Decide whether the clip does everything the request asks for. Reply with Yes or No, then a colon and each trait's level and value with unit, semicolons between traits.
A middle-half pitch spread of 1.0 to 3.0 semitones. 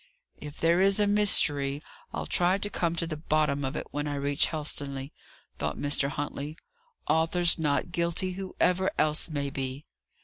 No: average, 3.5 semitones